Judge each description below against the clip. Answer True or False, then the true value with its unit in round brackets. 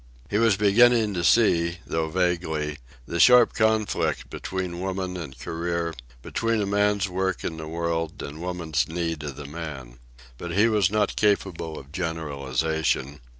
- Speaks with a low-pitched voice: True (85 Hz)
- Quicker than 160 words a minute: False (150 wpm)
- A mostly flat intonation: False (4.1 semitones)